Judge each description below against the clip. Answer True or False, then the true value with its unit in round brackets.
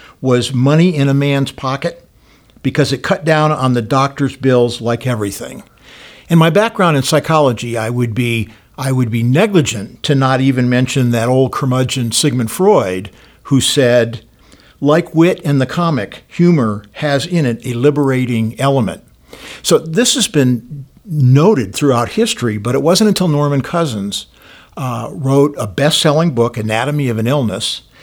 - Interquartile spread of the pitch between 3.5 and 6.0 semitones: True (4.0 semitones)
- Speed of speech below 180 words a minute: True (155 wpm)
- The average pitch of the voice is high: False (135 Hz)